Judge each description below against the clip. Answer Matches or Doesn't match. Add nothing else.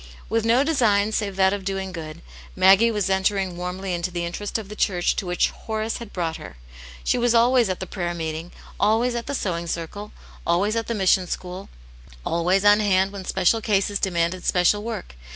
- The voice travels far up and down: Doesn't match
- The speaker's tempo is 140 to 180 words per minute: Doesn't match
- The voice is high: Matches